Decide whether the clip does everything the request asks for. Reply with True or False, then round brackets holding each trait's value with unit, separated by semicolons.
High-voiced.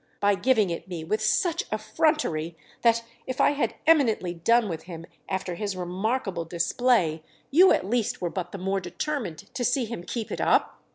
True (205 Hz)